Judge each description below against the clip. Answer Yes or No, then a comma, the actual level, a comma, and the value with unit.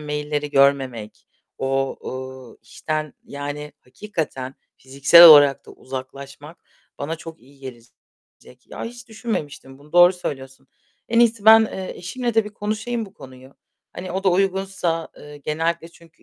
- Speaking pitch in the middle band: Yes, medium, 150 Hz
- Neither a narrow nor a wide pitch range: No, wide, 5.8 semitones